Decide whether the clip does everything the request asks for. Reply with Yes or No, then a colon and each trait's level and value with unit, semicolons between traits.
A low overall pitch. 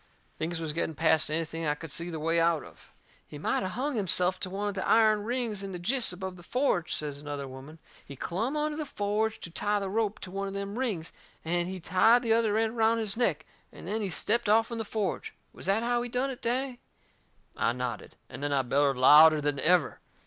No: high, 190 Hz